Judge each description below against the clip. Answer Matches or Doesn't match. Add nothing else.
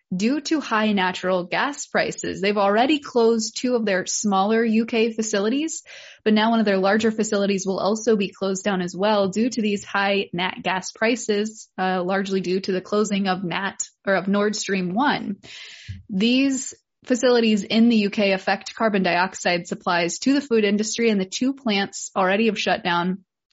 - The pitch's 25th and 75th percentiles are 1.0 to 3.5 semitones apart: Matches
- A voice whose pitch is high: Matches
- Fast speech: Doesn't match